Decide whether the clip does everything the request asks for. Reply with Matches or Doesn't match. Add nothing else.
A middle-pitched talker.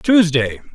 Matches